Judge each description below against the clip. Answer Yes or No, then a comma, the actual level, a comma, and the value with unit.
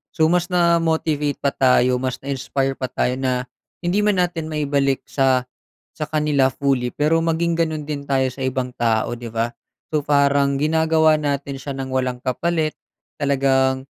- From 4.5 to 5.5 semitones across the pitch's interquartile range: No, average, 3.1 semitones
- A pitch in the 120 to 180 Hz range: Yes, medium, 140 Hz